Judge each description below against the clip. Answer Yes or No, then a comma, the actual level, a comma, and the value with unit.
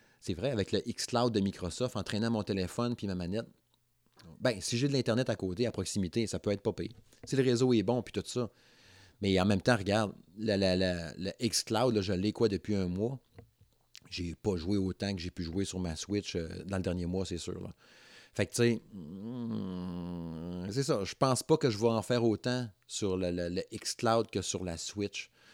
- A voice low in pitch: Yes, low, 105 Hz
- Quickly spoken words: Yes, fast, 230 wpm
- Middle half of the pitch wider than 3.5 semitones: Yes, average, 4.2 semitones